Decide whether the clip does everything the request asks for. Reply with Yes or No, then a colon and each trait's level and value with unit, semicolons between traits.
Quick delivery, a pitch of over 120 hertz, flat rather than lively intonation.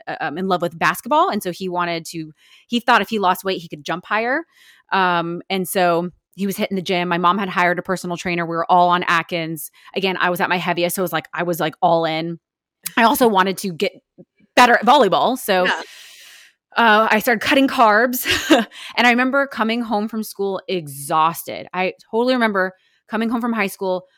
No: fast, 210 wpm; high, 190 Hz; average, 4.9 semitones